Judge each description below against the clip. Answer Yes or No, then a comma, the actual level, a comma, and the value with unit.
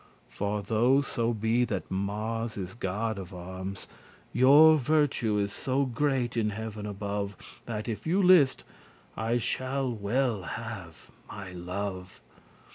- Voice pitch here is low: Yes, low, 110 Hz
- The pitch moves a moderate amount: Yes, average, 4.0 semitones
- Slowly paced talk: Yes, slow, 130 wpm